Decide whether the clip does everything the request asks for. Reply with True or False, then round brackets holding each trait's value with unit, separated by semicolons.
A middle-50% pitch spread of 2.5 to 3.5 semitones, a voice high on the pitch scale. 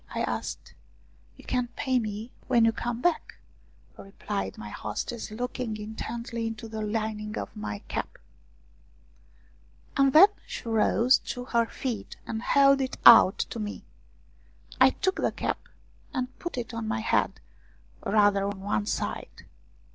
True (3.0 semitones; 225 Hz)